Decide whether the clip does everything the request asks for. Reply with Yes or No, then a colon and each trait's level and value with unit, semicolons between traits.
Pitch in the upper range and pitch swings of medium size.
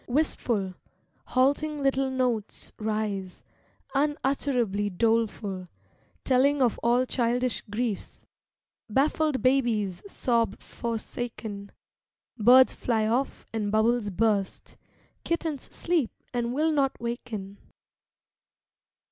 Yes: high, 240 Hz; average, 3.9 semitones